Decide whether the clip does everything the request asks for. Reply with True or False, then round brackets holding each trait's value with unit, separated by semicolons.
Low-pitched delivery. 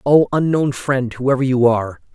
True (130 Hz)